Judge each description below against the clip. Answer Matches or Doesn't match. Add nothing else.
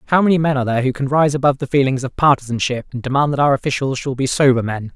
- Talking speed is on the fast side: Matches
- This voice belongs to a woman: Doesn't match